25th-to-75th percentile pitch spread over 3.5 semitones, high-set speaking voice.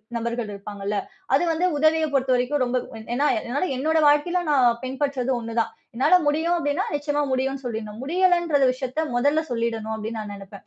Yes: average, 4.4 semitones; very high, 265 Hz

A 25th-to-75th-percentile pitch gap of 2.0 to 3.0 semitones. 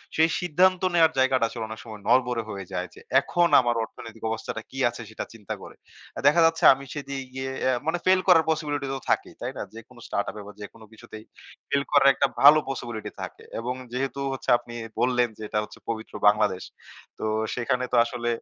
No: average, 4.2 semitones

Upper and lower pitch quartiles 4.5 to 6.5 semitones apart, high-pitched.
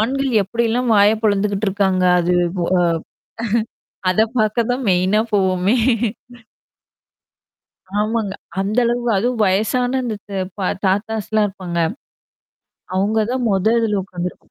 No: average, 3.2 semitones; high, 205 Hz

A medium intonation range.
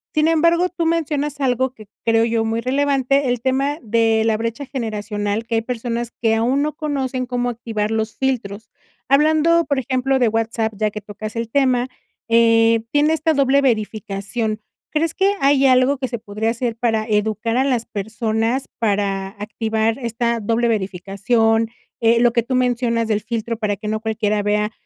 Yes: average, 3.3 semitones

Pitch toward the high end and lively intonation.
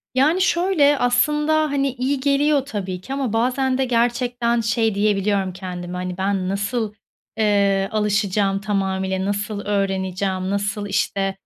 No: high, 210 Hz; average, 4.9 semitones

